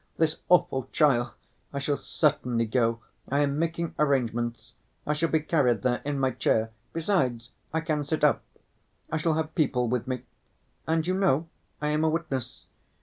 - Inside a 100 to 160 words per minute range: No, average, 170 wpm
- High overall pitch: No, medium, 145 Hz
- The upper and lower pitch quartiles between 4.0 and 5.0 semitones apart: Yes, average, 4.4 semitones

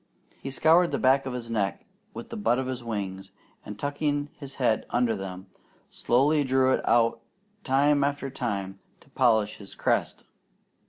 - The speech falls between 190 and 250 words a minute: No, average, 165 wpm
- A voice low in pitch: Yes, low, 125 Hz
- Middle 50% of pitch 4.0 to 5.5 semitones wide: Yes, average, 4.5 semitones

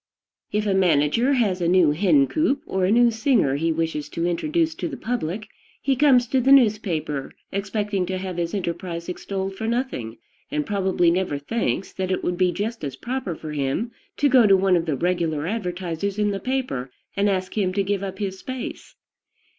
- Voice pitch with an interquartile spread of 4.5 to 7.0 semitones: Yes, average, 4.9 semitones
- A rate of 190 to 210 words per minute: Yes, average, 195 wpm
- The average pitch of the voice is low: No, high, 190 Hz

